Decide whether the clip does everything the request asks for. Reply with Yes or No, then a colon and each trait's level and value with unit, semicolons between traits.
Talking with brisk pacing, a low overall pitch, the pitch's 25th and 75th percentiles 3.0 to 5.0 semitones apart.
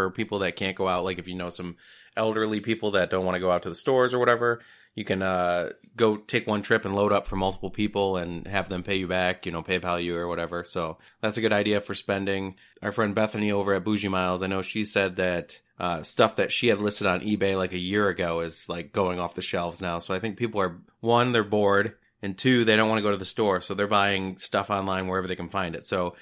No: fast, 265 wpm; very low, 95 Hz; narrow, 2.5 semitones